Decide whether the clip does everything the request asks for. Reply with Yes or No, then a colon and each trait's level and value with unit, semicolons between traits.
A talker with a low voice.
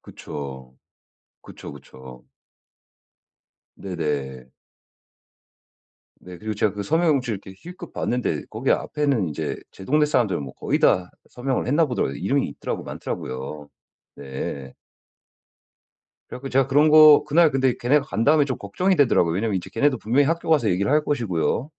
Yes: low, 120 Hz